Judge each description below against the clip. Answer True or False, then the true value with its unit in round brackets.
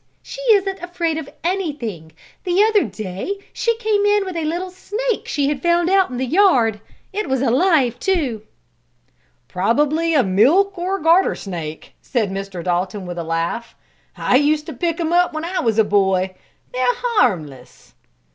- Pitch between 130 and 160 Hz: False (300 Hz)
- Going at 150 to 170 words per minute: True (165 wpm)